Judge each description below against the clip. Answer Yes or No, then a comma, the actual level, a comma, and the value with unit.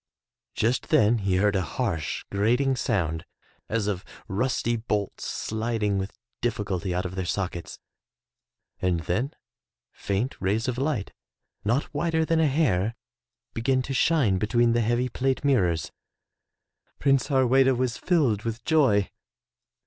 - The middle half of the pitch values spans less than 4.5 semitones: No, average, 5.0 semitones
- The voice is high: No, low, 115 Hz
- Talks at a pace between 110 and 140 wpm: Yes, slow, 135 wpm